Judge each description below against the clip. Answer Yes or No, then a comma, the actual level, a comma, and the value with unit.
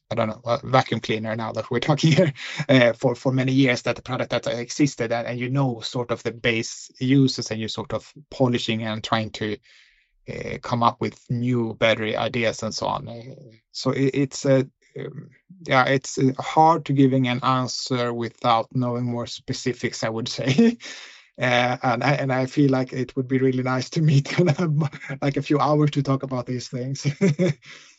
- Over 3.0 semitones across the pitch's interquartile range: No, average, 2.7 semitones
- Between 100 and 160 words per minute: No, average, 190 wpm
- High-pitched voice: No, low, 130 Hz